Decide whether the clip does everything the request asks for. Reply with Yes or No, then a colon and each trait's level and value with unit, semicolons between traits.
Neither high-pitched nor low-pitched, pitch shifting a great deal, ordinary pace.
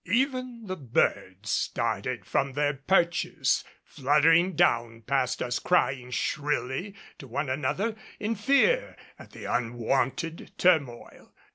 No: medium, 145 Hz; wide, 6.9 semitones; slow, 115 wpm